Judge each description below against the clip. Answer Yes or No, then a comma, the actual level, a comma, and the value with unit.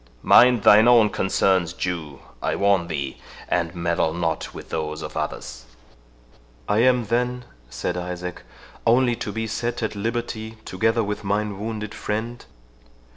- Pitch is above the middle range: No, low, 105 Hz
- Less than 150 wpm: Yes, average, 140 wpm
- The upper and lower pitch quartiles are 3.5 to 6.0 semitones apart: Yes, average, 4.6 semitones